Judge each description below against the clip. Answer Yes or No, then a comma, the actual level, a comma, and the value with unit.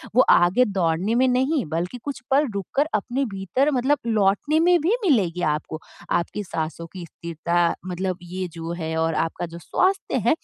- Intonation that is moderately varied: No, wide, 7.6 semitones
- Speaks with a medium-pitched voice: No, high, 195 Hz